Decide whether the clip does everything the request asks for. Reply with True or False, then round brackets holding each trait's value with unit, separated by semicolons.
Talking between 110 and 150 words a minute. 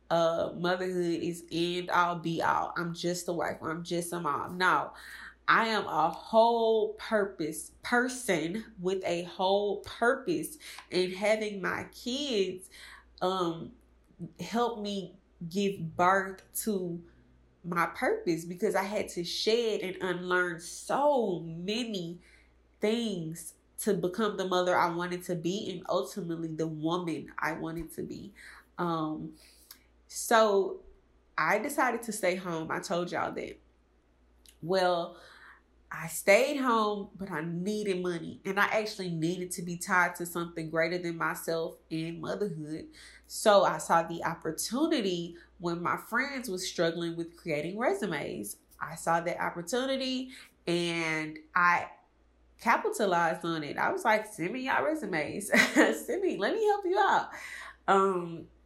True (135 wpm)